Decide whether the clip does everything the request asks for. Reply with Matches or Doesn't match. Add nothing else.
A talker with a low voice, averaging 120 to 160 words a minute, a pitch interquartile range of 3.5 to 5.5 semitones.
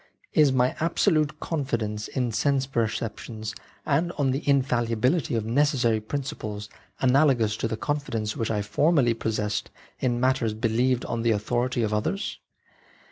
Matches